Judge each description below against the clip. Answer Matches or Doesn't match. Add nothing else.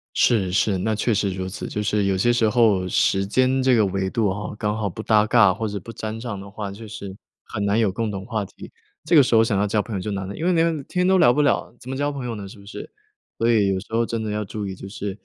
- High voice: Doesn't match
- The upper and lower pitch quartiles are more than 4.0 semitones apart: Doesn't match